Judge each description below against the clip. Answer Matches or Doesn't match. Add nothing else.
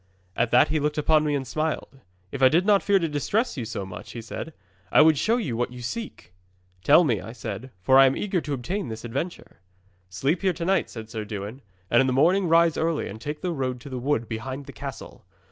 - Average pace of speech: Doesn't match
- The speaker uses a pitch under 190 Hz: Matches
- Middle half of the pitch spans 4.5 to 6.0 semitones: Matches